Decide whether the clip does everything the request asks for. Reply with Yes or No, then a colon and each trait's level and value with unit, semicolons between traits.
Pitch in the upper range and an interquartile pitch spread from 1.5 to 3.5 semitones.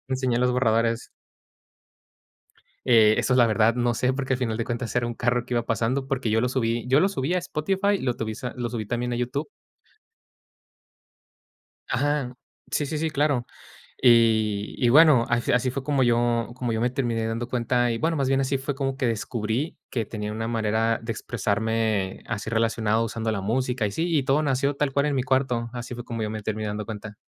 No: low, 120 Hz; average, 2.8 semitones